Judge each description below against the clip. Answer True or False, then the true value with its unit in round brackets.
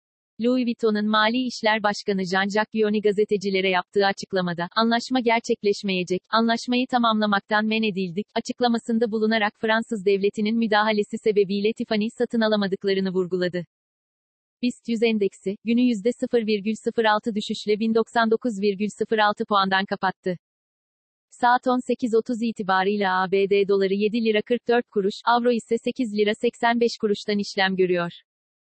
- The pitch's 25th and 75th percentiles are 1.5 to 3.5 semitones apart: True (2.5 semitones)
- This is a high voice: True (215 Hz)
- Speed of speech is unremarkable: True (110 wpm)